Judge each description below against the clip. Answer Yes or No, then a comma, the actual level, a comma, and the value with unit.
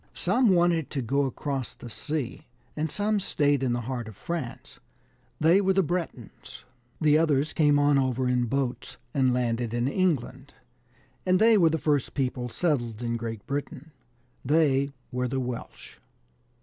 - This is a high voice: No, medium, 140 Hz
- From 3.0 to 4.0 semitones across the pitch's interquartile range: No, average, 4.4 semitones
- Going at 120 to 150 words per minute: No, average, 160 wpm